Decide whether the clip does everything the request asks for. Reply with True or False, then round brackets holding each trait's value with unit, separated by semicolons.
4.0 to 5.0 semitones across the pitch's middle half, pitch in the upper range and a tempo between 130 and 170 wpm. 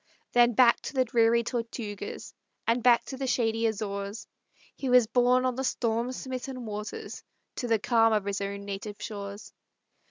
False (3.0 semitones; 230 Hz; 165 wpm)